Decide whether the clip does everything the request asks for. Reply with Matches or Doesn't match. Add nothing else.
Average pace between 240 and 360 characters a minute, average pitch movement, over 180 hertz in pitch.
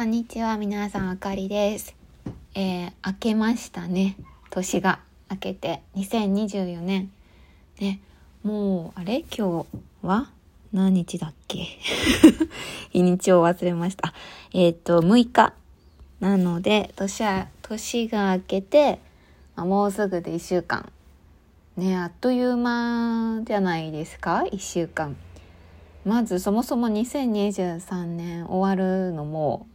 Doesn't match